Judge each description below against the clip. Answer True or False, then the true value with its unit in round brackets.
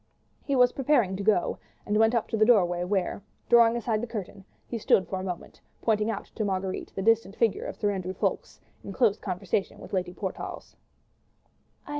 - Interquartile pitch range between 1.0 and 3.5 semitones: True (3.2 semitones)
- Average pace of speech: True (190 wpm)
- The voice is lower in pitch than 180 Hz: False (205 Hz)